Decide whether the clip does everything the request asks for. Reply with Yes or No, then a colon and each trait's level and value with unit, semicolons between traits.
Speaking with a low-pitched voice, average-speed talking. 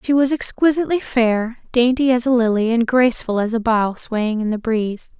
No: high, 240 Hz; average, 195 wpm